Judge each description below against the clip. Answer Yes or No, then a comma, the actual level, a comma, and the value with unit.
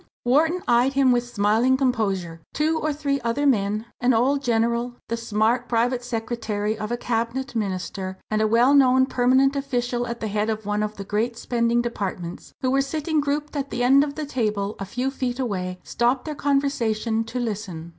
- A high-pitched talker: Yes, high, 240 Hz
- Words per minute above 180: Yes, average, 195 wpm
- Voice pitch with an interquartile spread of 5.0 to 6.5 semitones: No, average, 3.7 semitones